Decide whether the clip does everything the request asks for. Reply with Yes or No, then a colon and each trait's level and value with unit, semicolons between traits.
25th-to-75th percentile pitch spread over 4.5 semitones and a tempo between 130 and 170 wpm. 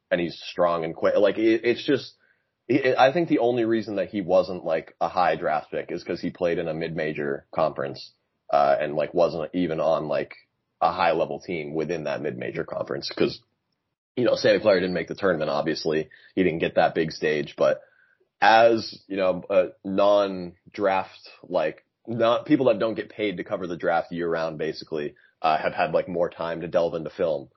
No: average, 5.1 semitones; average, 195 wpm